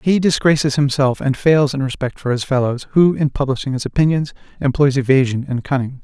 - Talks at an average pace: Yes, average, 190 wpm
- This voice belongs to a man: Yes, male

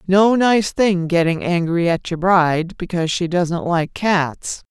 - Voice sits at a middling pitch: Yes, medium, 180 Hz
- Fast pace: No, average, 165 wpm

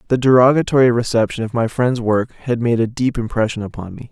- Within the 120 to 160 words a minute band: No, fast, 205 wpm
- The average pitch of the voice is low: Yes, low, 120 Hz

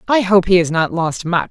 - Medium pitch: Yes, medium, 180 Hz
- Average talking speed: No, fast, 280 wpm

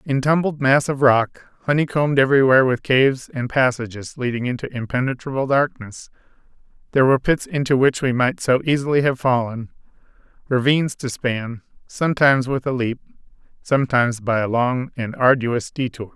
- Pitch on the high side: No, low, 130 Hz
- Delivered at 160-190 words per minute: No, average, 150 wpm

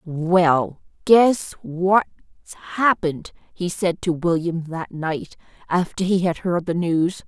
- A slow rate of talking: Yes, slow, 130 wpm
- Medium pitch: Yes, medium, 175 Hz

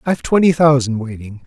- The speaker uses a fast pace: No, average, 165 wpm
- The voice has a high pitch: No, low, 135 Hz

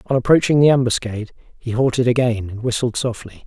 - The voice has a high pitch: No, low, 120 Hz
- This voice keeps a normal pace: Yes, average, 175 wpm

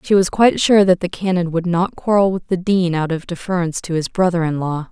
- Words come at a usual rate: No, fast, 255 wpm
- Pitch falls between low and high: Yes, medium, 180 Hz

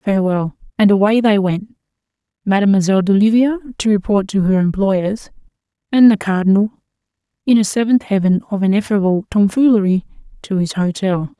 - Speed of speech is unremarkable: No, slow, 125 wpm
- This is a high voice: Yes, high, 200 Hz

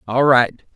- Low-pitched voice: Yes, low, 125 Hz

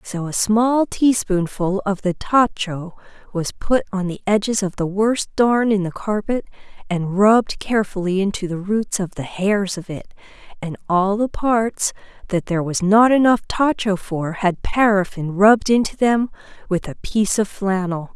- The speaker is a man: No, female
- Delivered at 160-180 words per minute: Yes, average, 170 wpm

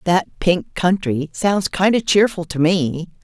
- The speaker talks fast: No, average, 165 wpm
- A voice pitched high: No, medium, 180 Hz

